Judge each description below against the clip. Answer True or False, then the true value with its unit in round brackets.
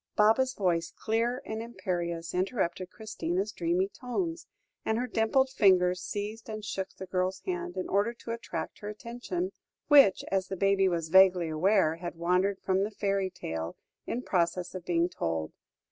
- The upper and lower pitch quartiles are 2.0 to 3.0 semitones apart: False (3.7 semitones)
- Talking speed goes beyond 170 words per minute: False (160 wpm)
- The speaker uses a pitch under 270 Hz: True (190 Hz)